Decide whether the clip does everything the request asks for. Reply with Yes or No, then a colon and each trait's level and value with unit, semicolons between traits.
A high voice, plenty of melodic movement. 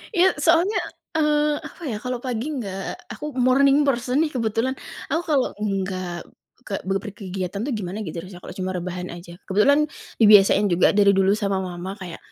Yes: high, 205 Hz; wide, 5.8 semitones